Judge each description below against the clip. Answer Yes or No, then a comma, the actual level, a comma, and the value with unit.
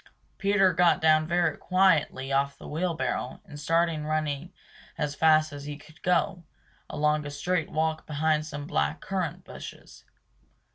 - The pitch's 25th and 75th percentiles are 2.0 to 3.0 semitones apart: Yes, average, 2.7 semitones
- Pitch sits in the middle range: Yes, medium, 155 Hz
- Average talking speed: Yes, average, 150 wpm